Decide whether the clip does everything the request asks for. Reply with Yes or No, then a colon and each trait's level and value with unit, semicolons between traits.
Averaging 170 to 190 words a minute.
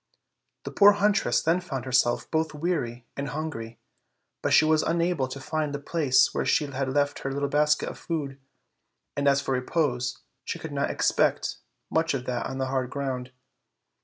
Yes: average, 185 wpm